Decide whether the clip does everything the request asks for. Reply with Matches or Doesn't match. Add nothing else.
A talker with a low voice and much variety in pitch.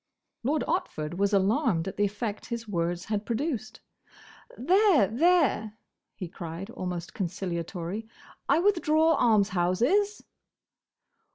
Doesn't match